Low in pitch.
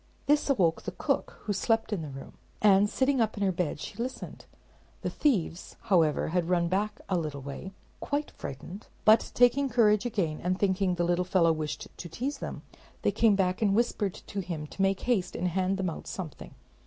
No: high, 190 Hz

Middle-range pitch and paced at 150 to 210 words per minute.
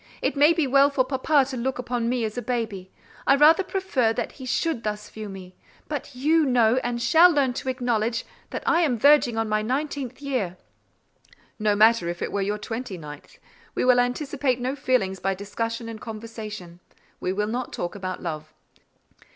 No: high, 240 Hz; average, 190 wpm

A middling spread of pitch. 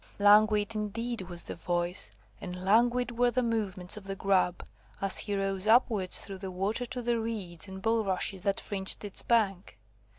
Yes: average, 3.1 semitones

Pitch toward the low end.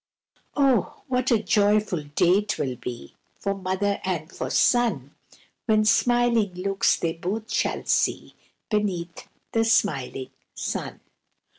No: high, 200 Hz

